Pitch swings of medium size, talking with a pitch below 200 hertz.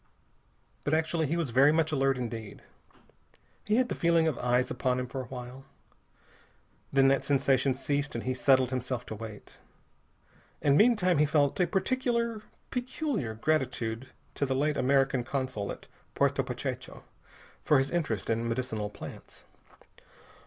Yes: average, 4.1 semitones; low, 135 Hz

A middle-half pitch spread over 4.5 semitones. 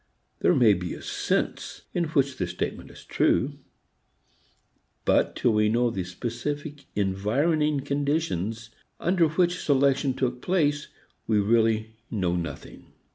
Yes: wide, 5.5 semitones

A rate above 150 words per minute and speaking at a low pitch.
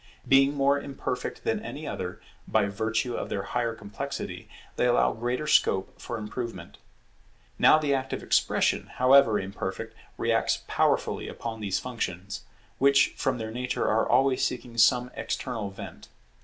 No: average, 145 wpm; low, 120 Hz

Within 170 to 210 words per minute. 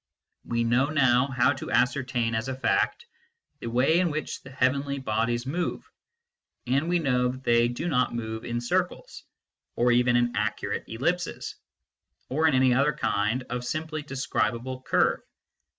No: average, 160 wpm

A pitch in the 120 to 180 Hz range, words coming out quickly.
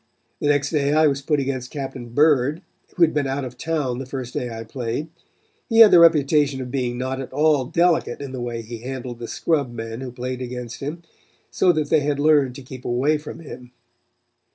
Yes: low, 135 Hz; fast, 215 wpm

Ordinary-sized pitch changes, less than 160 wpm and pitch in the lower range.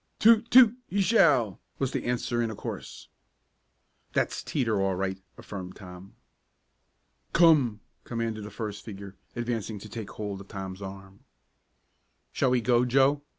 Yes: average, 4.5 semitones; average, 145 wpm; low, 110 Hz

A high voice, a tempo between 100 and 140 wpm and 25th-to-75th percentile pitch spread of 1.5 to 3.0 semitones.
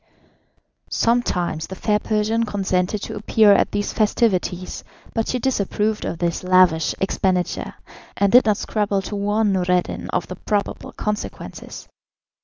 Yes: high, 205 Hz; slow, 135 wpm; average, 2.7 semitones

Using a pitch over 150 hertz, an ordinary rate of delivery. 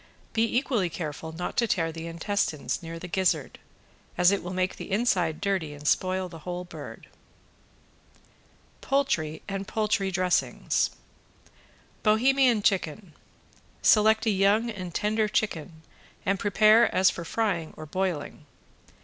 No: medium, 185 Hz; slow, 130 wpm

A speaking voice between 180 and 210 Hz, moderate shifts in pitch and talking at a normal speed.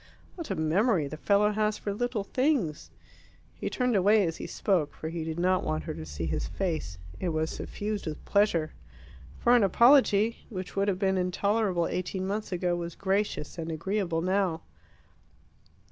Yes: high, 190 Hz; average, 4.3 semitones; average, 175 wpm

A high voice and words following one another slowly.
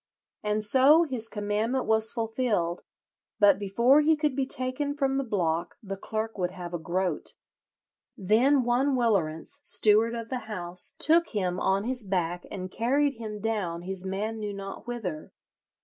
No: high, 215 Hz; average, 160 wpm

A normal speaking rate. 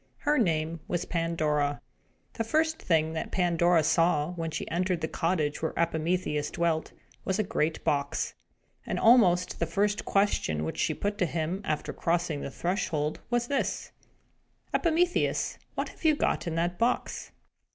Yes: average, 150 wpm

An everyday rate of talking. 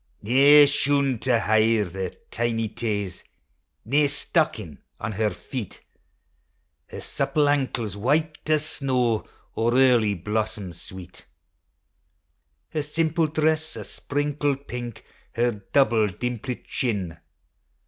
No: slow, 105 wpm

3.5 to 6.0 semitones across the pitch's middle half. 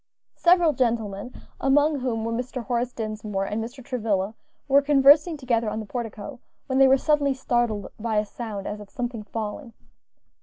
Yes: average, 3.9 semitones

